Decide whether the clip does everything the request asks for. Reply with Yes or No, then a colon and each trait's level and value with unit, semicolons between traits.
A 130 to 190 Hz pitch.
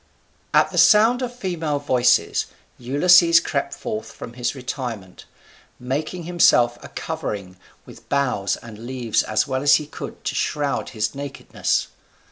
Yes: medium, 140 Hz